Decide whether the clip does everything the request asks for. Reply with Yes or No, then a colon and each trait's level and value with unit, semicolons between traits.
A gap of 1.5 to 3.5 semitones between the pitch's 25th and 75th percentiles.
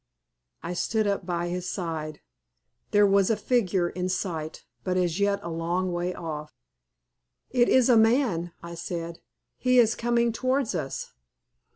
No: average, 4.7 semitones